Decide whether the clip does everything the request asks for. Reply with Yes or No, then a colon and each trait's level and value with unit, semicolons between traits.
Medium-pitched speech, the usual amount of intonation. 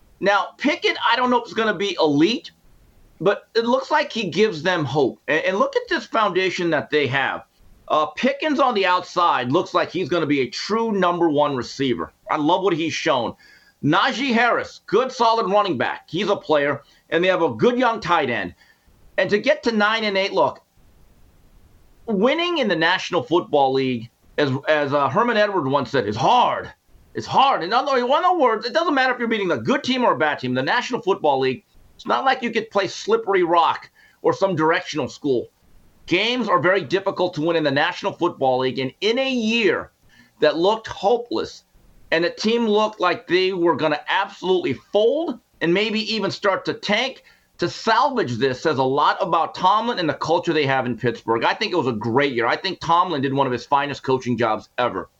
No: medium, 180 Hz; wide, 7.7 semitones